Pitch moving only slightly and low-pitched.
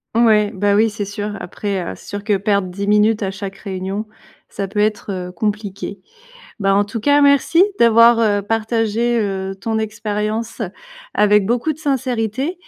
No: narrow, 2.2 semitones; high, 210 Hz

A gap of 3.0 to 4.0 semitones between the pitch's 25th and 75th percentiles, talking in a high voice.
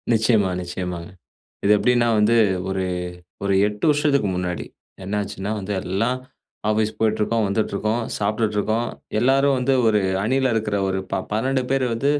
No: average, 3.5 semitones; low, 110 Hz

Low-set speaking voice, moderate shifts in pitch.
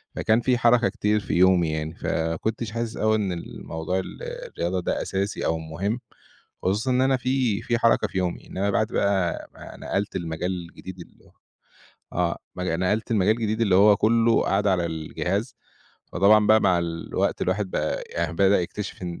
Yes: low, 100 Hz; average, 3.7 semitones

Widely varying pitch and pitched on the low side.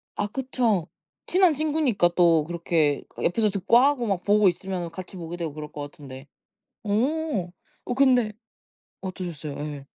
No: wide, 6.7 semitones; high, 190 Hz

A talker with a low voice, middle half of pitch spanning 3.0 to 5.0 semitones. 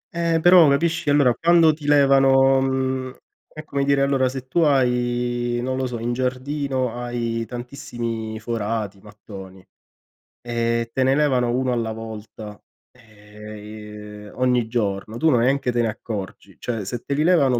Yes: low, 125 Hz; average, 3.3 semitones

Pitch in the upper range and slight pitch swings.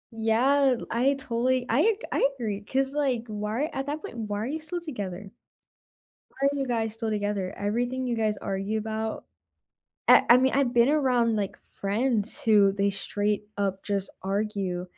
No: high, 225 Hz; average, 4.1 semitones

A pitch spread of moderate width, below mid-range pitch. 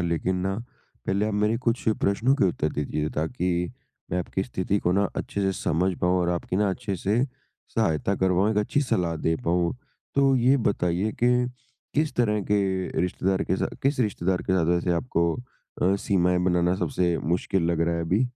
Yes: average, 3.3 semitones; very low, 95 Hz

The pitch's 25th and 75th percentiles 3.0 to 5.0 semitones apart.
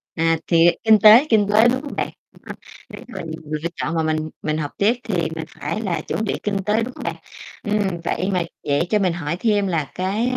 Yes: average, 4.6 semitones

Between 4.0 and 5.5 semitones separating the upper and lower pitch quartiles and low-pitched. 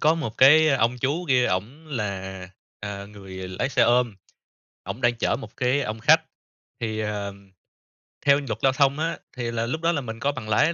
Yes: average, 4.8 semitones; low, 120 Hz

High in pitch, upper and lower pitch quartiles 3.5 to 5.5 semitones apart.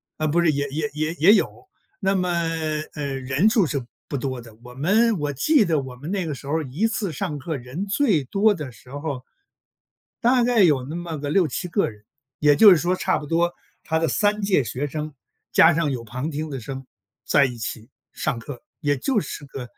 No: medium, 150 Hz; average, 5.2 semitones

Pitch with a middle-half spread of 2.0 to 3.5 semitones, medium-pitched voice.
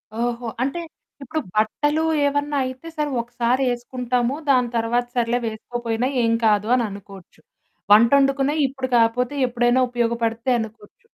No: narrow, 2.6 semitones; high, 240 Hz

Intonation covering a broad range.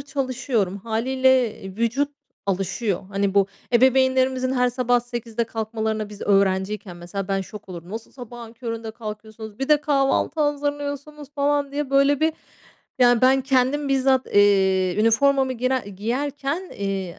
No: average, 4.7 semitones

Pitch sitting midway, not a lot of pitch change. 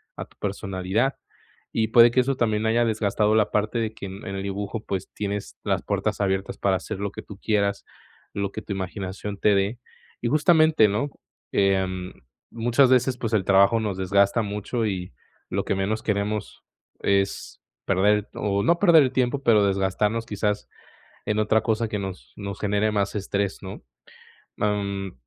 No: low, 105 Hz; narrow, 2.3 semitones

